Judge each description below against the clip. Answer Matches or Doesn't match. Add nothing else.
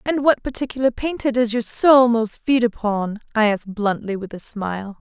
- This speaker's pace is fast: Doesn't match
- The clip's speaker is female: Matches